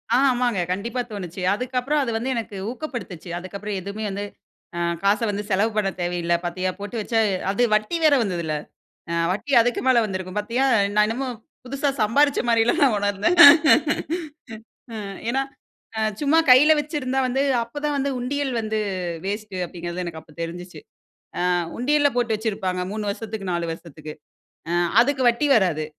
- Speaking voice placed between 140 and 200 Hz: No, high, 215 Hz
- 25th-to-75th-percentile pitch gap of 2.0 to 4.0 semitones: No, average, 5.1 semitones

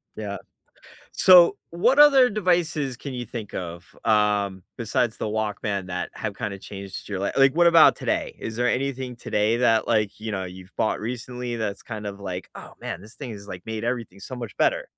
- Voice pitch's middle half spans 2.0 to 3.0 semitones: No, average, 4.3 semitones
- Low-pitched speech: Yes, low, 110 Hz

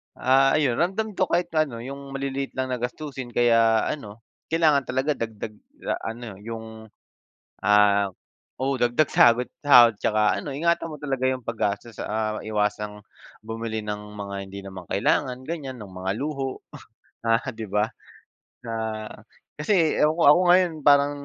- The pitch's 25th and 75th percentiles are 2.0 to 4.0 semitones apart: No, average, 4.8 semitones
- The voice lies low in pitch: Yes, low, 120 Hz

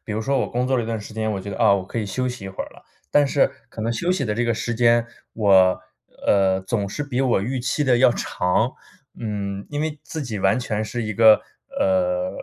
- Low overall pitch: Yes, low, 115 Hz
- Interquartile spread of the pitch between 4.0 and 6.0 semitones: Yes, average, 4.4 semitones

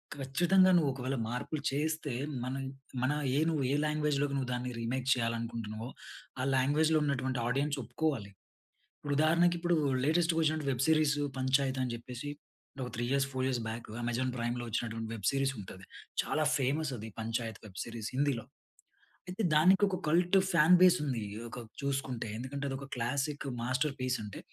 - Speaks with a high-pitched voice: No, low, 135 Hz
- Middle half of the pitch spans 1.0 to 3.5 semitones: No, average, 4.0 semitones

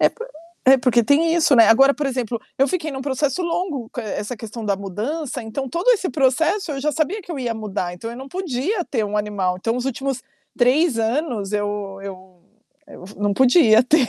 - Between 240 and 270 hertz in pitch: Yes, very high, 255 Hz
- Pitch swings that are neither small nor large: No, wide, 5.7 semitones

